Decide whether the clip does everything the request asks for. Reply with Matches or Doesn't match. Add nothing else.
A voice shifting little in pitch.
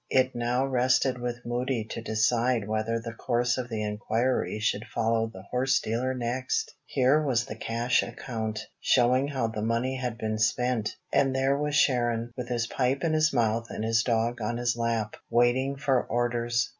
Matches